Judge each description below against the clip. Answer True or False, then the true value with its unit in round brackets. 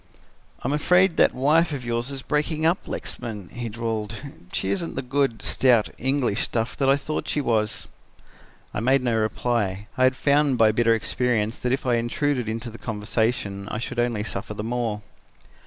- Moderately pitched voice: False (120 Hz)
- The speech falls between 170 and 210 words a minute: True (180 wpm)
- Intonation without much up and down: False (3.6 semitones)